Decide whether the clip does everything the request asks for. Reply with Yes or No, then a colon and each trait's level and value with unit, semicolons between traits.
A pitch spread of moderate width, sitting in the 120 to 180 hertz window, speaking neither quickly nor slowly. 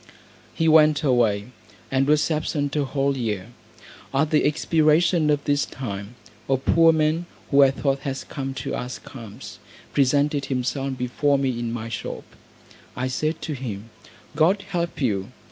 Yes: average, 3.4 semitones; medium, 140 Hz; average, 155 wpm